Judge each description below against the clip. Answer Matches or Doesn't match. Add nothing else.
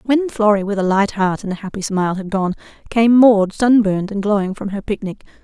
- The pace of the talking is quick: Matches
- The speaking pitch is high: Matches